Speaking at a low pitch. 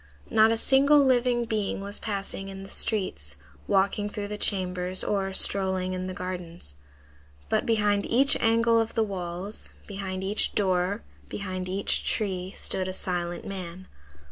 No: high, 195 Hz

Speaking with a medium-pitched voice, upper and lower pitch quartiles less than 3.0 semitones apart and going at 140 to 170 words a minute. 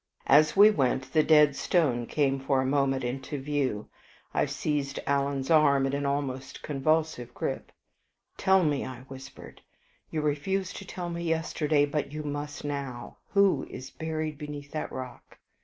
Yes: medium, 145 Hz; narrow, 2.4 semitones; average, 155 wpm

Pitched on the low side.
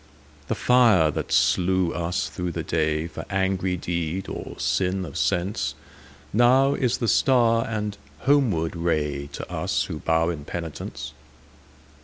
Yes: very low, 90 Hz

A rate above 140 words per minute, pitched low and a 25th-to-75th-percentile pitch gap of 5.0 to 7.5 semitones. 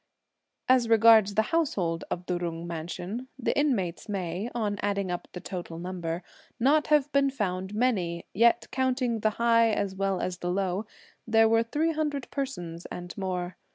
No: average, 165 wpm; high, 205 Hz; average, 5.3 semitones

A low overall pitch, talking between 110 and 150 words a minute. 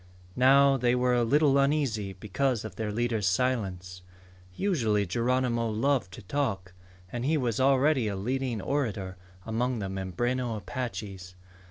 Yes: low, 120 Hz; average, 140 wpm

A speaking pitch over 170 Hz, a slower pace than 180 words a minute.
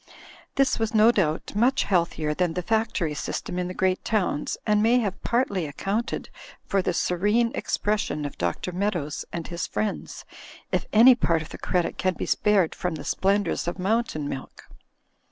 Yes: high, 190 Hz; average, 170 wpm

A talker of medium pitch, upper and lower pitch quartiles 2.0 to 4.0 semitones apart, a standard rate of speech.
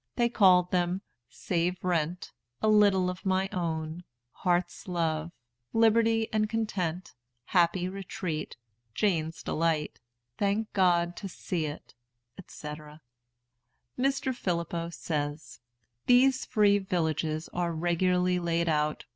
No: medium, 180 Hz; average, 3.2 semitones; slow, 110 wpm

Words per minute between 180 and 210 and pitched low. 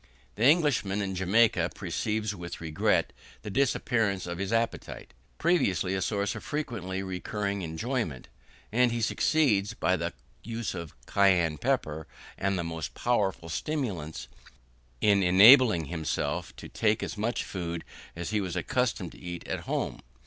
No: average, 145 wpm; low, 100 Hz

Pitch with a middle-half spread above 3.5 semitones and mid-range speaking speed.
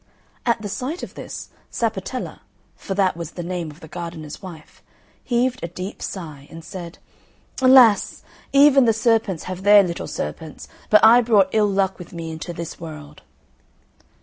Yes: average, 5.0 semitones; average, 165 wpm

